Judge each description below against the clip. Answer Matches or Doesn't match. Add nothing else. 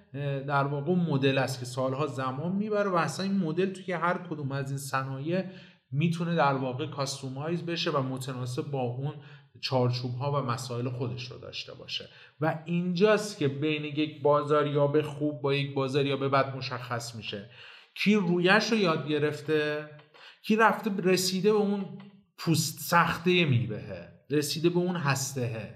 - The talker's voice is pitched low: Doesn't match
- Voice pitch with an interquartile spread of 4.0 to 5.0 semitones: Matches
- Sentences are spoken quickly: Matches